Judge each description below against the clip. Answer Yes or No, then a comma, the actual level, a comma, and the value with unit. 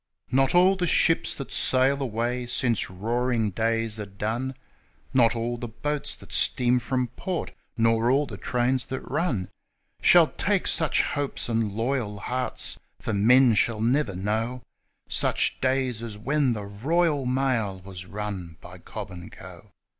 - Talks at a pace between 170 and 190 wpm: No, average, 155 wpm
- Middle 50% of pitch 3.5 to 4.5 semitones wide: Yes, average, 3.8 semitones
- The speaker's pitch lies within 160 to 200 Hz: No, low, 120 Hz